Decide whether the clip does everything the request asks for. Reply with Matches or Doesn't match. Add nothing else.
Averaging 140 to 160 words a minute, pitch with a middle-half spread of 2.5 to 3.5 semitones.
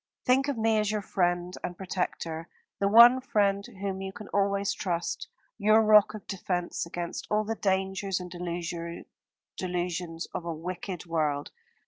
Matches